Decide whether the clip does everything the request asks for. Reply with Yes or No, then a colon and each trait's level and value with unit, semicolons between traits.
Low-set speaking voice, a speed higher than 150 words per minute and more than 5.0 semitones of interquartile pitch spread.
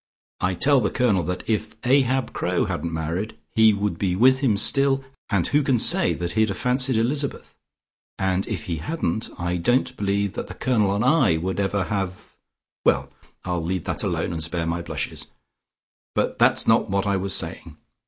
Yes: low, 100 Hz; average, 185 wpm; wide, 5.6 semitones